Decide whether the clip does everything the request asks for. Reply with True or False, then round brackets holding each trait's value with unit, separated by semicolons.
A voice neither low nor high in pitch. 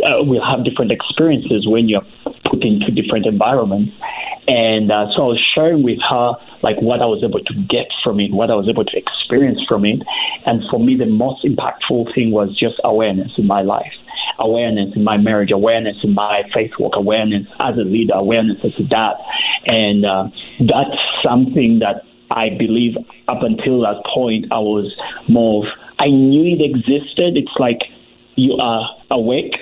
False (110 Hz)